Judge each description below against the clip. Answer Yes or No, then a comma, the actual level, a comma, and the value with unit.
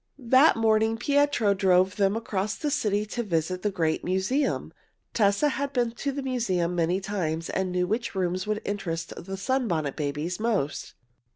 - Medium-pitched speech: No, high, 200 Hz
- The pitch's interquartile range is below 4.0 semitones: No, average, 4.6 semitones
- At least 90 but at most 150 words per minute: No, average, 165 wpm